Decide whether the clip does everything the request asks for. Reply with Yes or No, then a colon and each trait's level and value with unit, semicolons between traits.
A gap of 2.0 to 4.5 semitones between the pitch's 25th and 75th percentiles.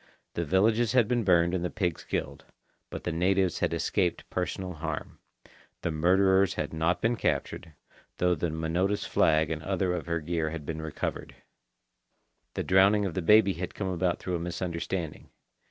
Yes: average, 2.7 semitones